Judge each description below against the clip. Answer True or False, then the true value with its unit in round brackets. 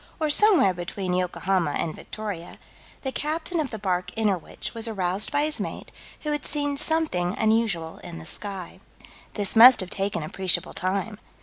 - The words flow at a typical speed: True (165 wpm)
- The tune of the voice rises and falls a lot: True (7.2 semitones)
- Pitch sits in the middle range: False (205 Hz)